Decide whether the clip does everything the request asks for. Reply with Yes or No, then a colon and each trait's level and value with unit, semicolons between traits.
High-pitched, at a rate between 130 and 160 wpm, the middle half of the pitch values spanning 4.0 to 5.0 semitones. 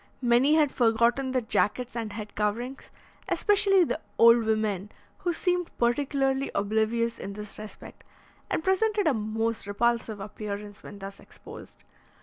Yes: high, 235 Hz; slow, 135 wpm; average, 4.4 semitones